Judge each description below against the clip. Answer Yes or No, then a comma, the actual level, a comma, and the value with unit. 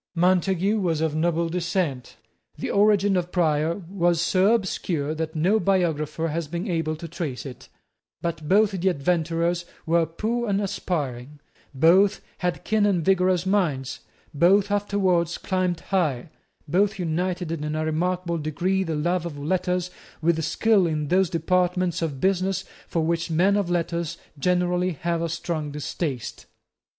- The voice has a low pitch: No, medium, 175 Hz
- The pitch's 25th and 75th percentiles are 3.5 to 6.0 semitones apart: No, average, 2.8 semitones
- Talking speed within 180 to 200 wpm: No, average, 145 wpm